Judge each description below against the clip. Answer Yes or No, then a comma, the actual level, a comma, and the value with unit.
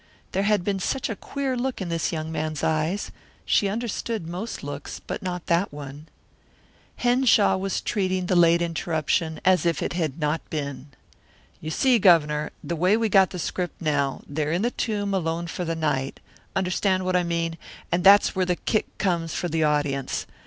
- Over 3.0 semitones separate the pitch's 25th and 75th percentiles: Yes, average, 3.7 semitones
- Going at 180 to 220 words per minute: Yes, average, 185 wpm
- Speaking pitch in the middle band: Yes, medium, 175 Hz